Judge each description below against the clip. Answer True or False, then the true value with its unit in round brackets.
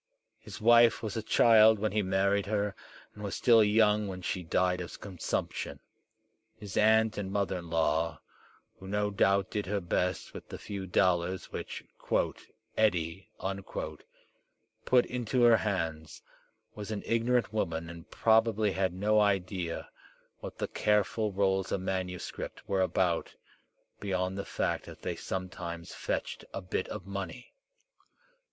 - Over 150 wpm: False (145 wpm)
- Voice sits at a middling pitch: False (100 Hz)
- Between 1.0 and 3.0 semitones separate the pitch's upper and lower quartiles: True (2.6 semitones)